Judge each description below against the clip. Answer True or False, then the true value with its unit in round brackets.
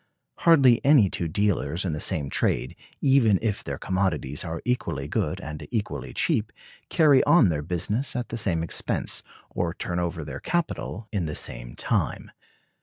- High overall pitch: False (95 Hz)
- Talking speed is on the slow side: False (165 wpm)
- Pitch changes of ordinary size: False (6.7 semitones)